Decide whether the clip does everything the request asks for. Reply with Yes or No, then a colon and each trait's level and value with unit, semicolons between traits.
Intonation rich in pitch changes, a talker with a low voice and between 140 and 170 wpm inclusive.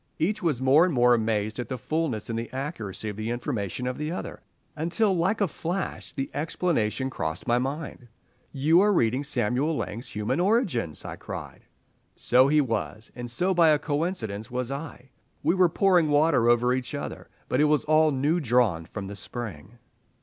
No: wide, 5.7 semitones; low, 130 Hz; average, 185 wpm